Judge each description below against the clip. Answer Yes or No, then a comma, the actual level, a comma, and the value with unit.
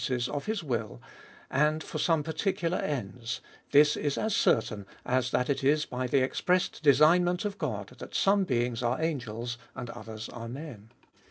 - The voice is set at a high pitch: No, low, 135 Hz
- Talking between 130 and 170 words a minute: No, average, 180 wpm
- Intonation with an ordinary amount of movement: Yes, average, 4.9 semitones